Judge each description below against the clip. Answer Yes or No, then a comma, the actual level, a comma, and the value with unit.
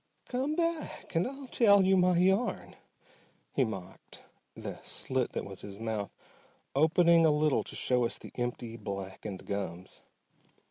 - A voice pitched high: No, medium, 140 Hz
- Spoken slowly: No, average, 145 wpm